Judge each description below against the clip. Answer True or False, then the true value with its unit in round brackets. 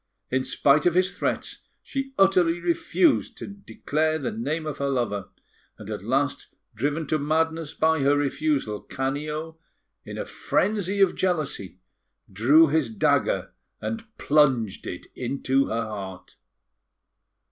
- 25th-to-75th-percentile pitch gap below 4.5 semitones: True (3.9 semitones)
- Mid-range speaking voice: True (150 Hz)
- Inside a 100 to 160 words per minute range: True (135 wpm)